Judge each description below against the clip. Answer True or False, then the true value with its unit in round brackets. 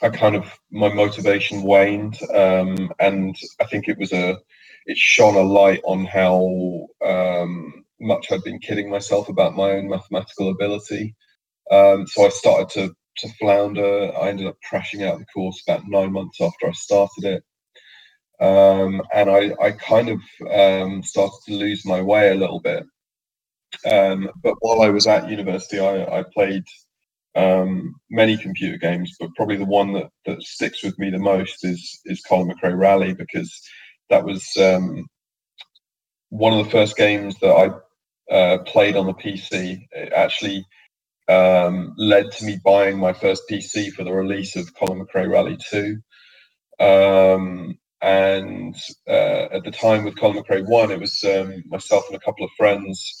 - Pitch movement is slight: True (1.4 semitones)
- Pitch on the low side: True (100 Hz)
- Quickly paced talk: False (170 wpm)